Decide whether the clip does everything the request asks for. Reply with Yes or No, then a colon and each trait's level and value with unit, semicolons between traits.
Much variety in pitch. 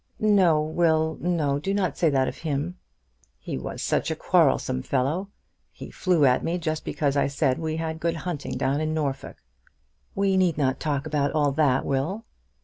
No: average, 3.4 semitones